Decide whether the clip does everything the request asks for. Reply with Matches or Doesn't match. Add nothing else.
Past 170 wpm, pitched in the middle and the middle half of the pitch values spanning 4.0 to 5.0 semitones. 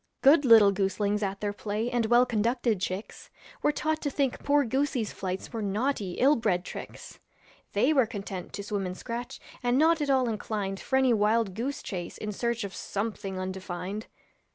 Doesn't match